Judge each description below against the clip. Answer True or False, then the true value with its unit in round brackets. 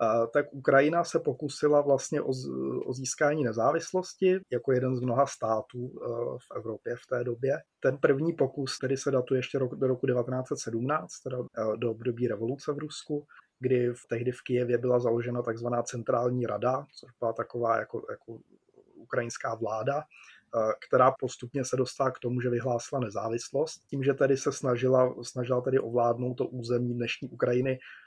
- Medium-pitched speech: False (125 Hz)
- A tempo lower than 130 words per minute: False (155 wpm)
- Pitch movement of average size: False (2.3 semitones)